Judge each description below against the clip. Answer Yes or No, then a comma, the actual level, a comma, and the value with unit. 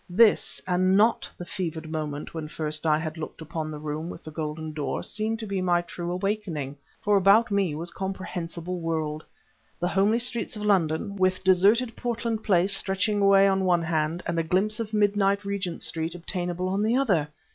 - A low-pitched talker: No, medium, 185 Hz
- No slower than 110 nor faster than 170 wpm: No, average, 190 wpm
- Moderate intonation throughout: Yes, average, 3.9 semitones